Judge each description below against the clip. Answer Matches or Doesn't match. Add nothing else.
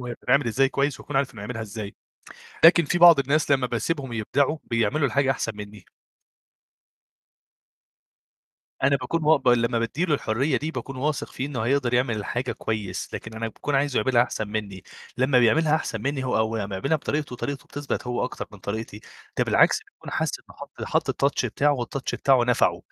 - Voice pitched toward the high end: Doesn't match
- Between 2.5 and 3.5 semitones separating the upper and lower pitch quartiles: Doesn't match